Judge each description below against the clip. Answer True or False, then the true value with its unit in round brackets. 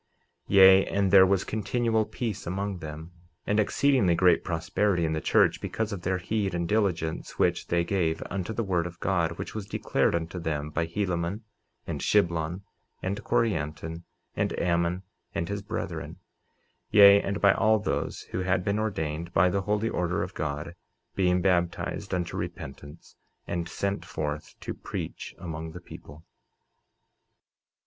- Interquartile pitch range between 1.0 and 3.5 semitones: True (3.2 semitones)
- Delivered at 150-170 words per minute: True (155 wpm)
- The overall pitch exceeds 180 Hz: False (90 Hz)